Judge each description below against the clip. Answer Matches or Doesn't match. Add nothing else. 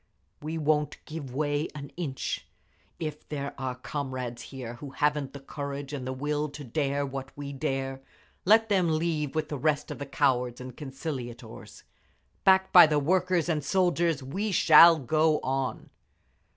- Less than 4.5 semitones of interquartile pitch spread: Matches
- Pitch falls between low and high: Matches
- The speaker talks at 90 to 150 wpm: Doesn't match